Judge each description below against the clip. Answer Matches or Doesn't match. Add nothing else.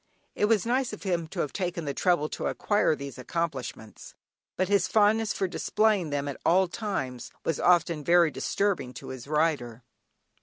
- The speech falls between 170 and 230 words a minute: Matches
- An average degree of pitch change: Doesn't match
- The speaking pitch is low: Doesn't match